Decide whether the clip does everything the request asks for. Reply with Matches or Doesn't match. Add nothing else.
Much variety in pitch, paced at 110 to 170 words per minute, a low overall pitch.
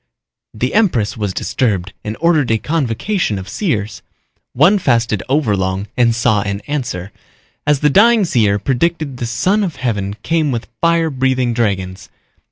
Matches